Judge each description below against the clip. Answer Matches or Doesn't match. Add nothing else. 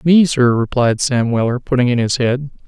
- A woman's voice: Doesn't match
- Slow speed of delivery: Doesn't match